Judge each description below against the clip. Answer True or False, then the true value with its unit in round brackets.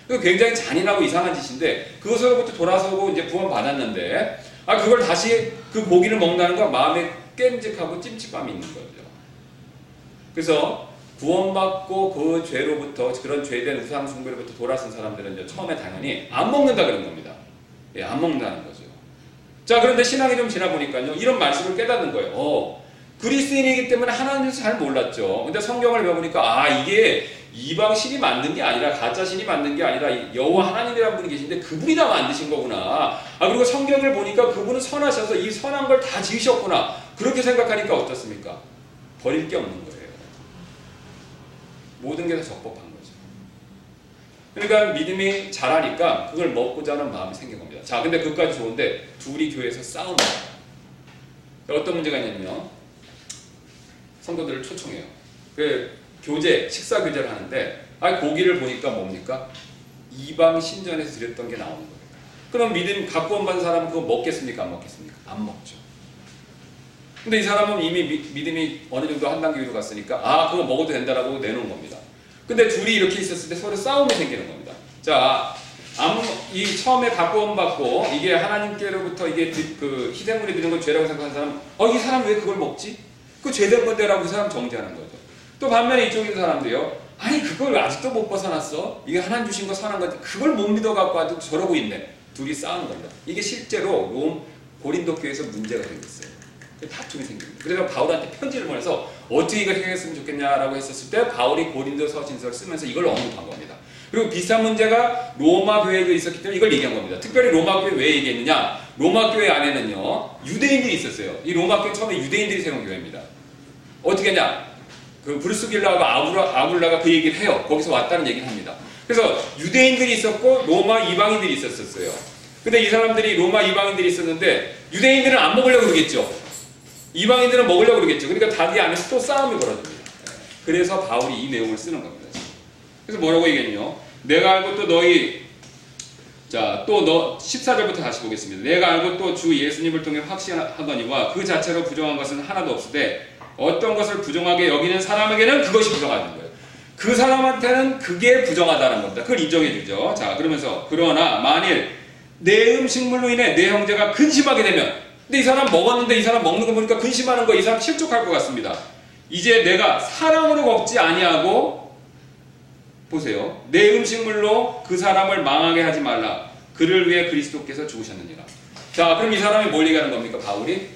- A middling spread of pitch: False (7.3 semitones)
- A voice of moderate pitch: False (195 Hz)